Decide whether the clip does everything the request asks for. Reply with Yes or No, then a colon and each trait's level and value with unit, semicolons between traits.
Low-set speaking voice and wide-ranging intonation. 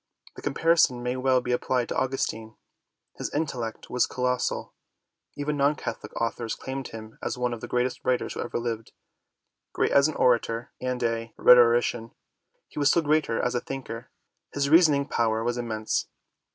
No: low, 125 Hz; average, 2.8 semitones